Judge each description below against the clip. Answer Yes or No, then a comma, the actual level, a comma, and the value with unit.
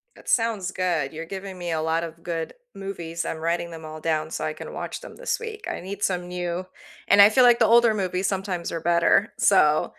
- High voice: No, medium, 180 Hz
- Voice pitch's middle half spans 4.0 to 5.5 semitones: No, average, 3.3 semitones